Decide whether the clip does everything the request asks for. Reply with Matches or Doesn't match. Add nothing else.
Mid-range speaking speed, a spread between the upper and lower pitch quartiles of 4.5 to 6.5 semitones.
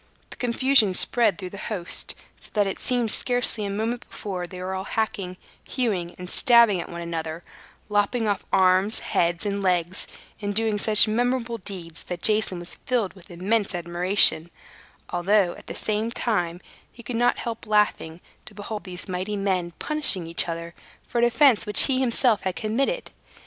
Doesn't match